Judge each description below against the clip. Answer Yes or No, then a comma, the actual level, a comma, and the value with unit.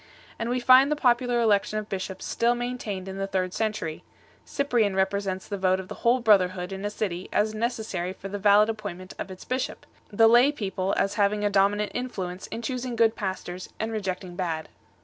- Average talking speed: No, fast, 210 wpm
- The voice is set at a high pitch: Yes, high, 205 Hz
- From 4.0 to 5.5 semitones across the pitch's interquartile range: No, average, 3.5 semitones